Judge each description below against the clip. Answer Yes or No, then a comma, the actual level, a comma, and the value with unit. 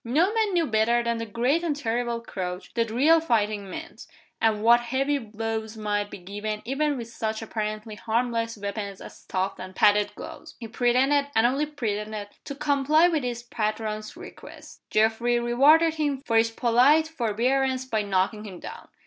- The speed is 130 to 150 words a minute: No, average, 170 wpm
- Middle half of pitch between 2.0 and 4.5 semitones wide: Yes, average, 4.1 semitones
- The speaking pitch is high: Yes, high, 230 Hz